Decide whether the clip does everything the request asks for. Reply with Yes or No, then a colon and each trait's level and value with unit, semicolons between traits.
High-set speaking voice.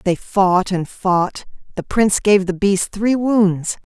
Yes: high, 195 Hz